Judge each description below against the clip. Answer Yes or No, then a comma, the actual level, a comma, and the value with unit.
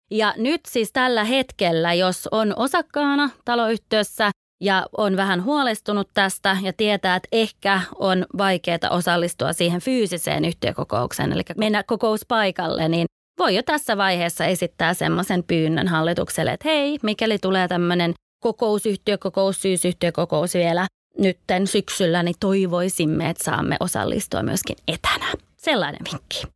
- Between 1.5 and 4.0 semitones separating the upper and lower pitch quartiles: Yes, average, 3.7 semitones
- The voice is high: Yes, high, 195 Hz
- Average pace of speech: Yes, average, 125 wpm